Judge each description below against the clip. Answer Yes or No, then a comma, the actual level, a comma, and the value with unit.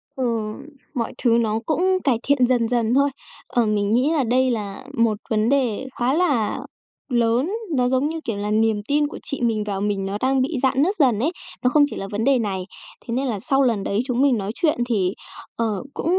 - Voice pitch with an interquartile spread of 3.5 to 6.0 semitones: Yes, average, 4.2 semitones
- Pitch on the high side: Yes, high, 240 Hz